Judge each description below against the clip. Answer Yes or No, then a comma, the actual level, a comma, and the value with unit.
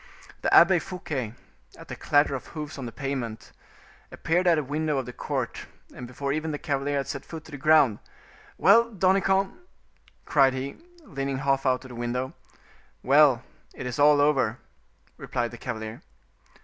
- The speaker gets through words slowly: No, average, 170 wpm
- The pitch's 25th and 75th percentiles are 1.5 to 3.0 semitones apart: No, average, 3.5 semitones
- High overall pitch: No, medium, 140 Hz